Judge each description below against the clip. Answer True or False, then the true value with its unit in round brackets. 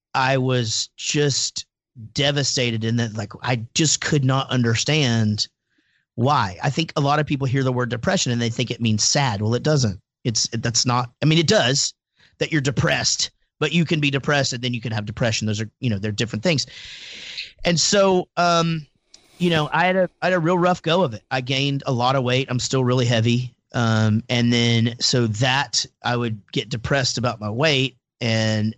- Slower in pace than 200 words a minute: False (205 wpm)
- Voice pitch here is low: True (125 Hz)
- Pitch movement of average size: True (4.0 semitones)